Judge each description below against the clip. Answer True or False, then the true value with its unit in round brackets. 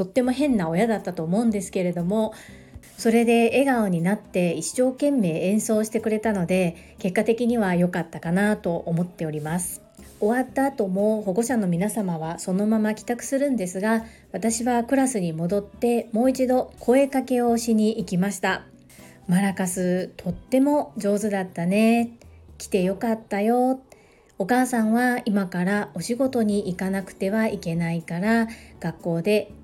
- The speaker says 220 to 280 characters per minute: False (320 characters per minute)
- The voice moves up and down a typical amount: True (4.3 semitones)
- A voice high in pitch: True (210 Hz)